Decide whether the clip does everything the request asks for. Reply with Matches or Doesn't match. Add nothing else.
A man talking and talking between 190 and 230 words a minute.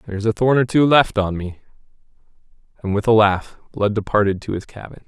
Matches